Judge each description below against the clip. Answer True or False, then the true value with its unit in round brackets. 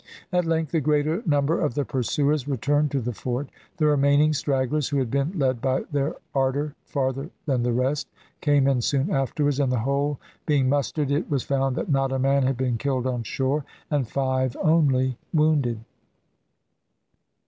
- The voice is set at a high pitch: False (140 Hz)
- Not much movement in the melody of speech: True (2.0 semitones)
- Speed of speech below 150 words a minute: False (175 wpm)